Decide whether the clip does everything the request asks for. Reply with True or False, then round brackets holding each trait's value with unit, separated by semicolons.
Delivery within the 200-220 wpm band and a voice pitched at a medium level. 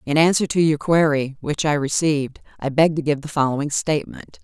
True (205 wpm; 150 Hz)